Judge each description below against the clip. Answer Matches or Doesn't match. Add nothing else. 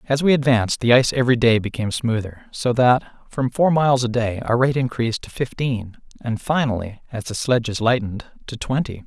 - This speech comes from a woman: Doesn't match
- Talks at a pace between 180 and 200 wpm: Matches